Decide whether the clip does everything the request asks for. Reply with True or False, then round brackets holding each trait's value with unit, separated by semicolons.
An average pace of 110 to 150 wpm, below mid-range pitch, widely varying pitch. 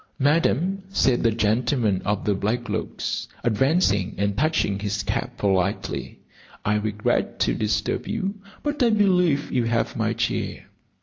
True (140 wpm; 115 Hz; 7.8 semitones)